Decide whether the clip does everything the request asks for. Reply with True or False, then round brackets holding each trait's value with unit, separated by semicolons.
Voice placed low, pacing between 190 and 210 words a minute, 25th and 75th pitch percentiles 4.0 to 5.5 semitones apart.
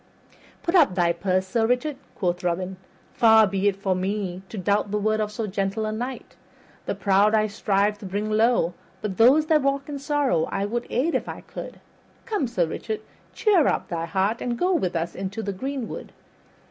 False (210 Hz; 200 wpm; 4.4 semitones)